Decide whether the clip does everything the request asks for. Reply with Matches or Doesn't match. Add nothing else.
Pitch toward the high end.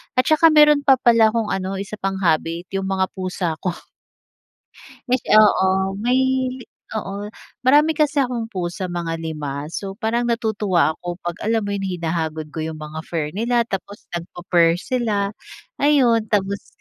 Matches